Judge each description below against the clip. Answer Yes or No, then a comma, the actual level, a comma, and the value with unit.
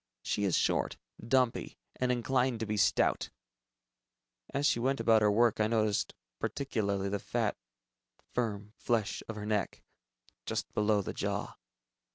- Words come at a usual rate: Yes, average, 145 wpm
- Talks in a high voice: No, low, 110 Hz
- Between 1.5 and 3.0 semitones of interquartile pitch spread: Yes, average, 2.7 semitones